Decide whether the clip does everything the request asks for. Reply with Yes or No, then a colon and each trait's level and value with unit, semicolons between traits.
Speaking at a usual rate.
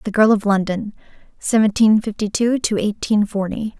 Yes: average, 160 wpm